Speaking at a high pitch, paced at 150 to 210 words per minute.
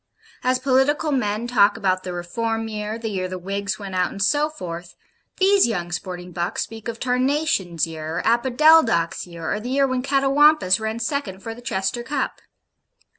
Yes: high, 225 Hz; average, 180 wpm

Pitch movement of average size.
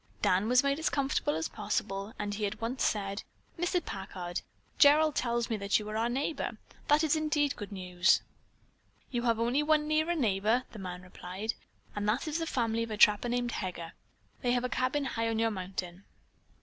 No: wide, 5.8 semitones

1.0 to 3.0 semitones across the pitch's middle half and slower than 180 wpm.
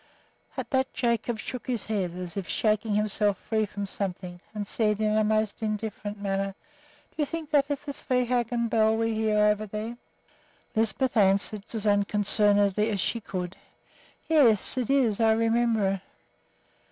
Yes: narrow, 2.4 semitones; average, 160 wpm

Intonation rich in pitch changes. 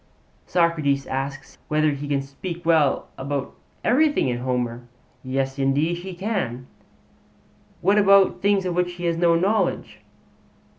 No: average, 4.9 semitones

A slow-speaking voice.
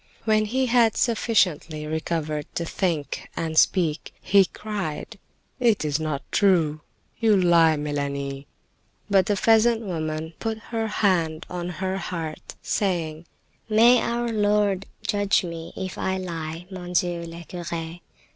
Yes: slow, 130 wpm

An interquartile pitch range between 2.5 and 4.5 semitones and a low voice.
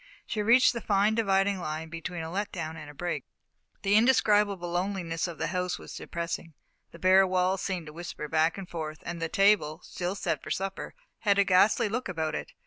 No: average, 3.3 semitones; medium, 185 Hz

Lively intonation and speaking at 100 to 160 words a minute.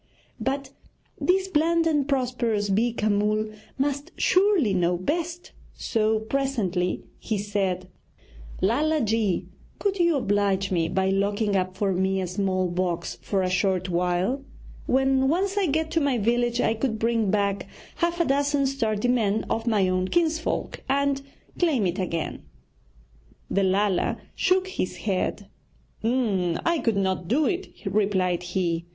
Yes: wide, 6.6 semitones; average, 145 wpm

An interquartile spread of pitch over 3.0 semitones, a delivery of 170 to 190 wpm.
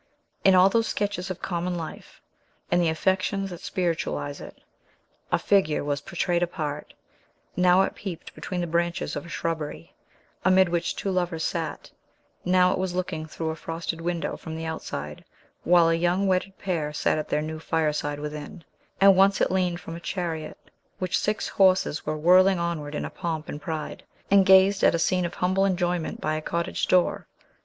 No: average, 2.7 semitones; average, 180 wpm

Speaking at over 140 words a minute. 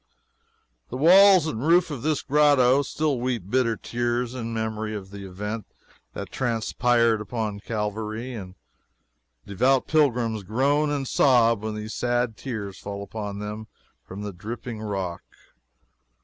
No: slow, 135 wpm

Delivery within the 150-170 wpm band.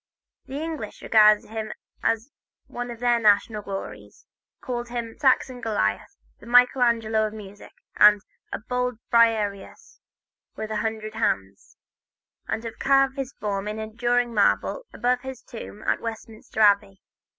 No: average, 140 wpm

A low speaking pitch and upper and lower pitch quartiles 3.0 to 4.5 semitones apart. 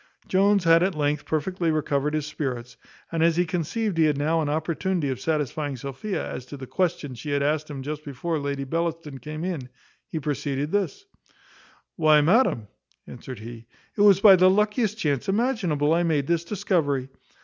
No: medium, 155 Hz; average, 4.0 semitones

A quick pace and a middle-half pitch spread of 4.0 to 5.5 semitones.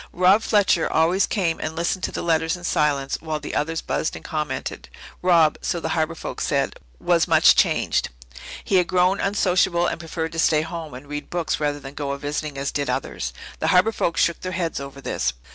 No: fast, 210 wpm; average, 3.2 semitones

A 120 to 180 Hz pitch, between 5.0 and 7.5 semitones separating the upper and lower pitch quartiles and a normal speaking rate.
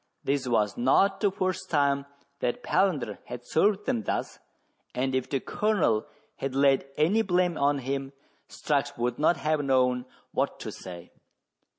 Yes: medium, 140 Hz; wide, 5.4 semitones; average, 155 wpm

